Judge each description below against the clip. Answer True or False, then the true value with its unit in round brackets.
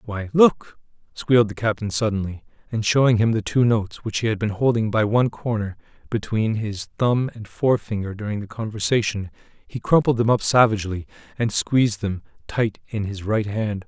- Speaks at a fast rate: False (175 wpm)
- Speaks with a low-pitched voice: True (110 Hz)